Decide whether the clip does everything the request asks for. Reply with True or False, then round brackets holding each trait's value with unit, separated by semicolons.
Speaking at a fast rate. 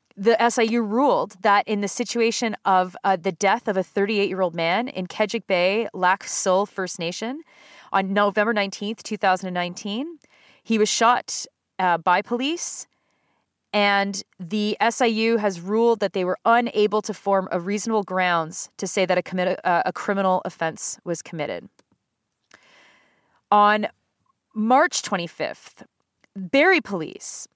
False (140 wpm)